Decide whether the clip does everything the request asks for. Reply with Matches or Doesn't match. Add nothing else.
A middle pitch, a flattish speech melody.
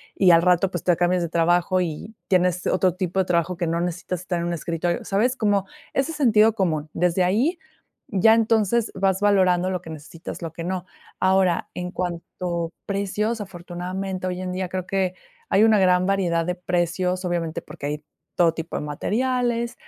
Matches